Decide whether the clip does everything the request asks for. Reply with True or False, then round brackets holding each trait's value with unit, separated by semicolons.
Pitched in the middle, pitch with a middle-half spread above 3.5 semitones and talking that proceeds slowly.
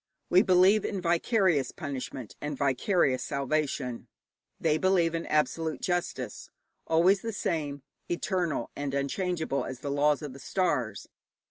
True (155 Hz; 4.5 semitones; 130 wpm)